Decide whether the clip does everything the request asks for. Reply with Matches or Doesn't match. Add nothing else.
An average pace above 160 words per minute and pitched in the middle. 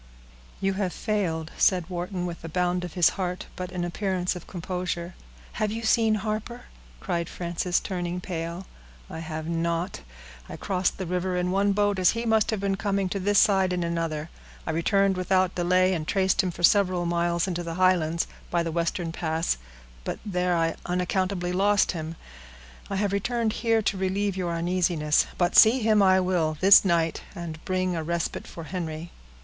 Matches